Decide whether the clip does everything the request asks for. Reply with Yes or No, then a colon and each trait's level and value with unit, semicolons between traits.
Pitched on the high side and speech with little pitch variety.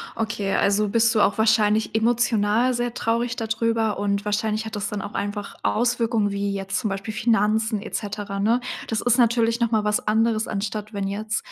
Yes: high, 215 Hz; narrow, 2.0 semitones